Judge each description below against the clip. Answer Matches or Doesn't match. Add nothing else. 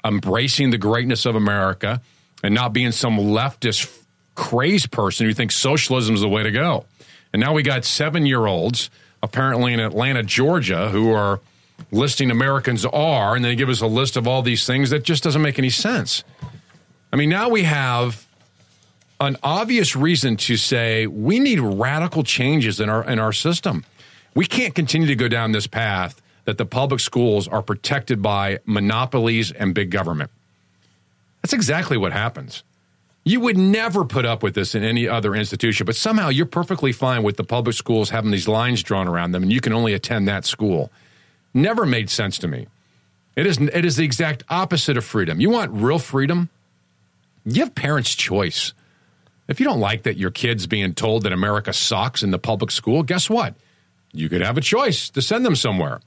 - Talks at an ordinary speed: Matches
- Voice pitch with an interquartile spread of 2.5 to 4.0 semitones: Doesn't match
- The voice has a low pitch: Matches